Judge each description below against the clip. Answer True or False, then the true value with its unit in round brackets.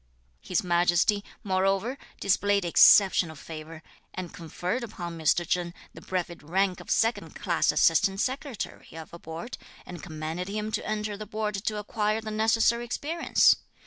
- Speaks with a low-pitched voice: False (195 Hz)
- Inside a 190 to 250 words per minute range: False (145 wpm)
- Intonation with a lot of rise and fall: False (3.9 semitones)